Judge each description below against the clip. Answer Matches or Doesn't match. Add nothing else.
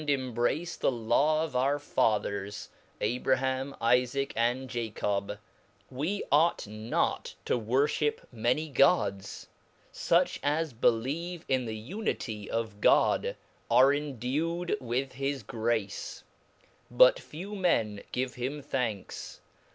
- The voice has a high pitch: Doesn't match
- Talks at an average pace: Doesn't match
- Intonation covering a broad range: Doesn't match